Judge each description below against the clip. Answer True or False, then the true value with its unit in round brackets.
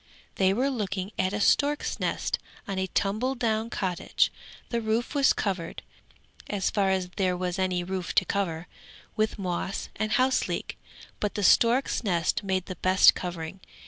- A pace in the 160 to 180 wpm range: True (165 wpm)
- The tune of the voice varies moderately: True (3.0 semitones)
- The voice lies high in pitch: True (195 Hz)